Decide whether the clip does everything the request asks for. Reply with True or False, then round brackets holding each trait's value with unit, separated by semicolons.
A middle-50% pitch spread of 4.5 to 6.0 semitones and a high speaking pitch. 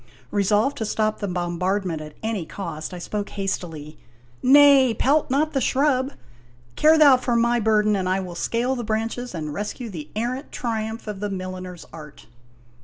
True (5.4 semitones; 210 Hz)